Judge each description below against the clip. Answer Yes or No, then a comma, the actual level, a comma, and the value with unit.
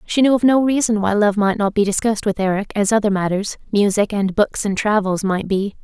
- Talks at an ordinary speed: No, fast, 215 wpm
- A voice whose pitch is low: No, high, 205 Hz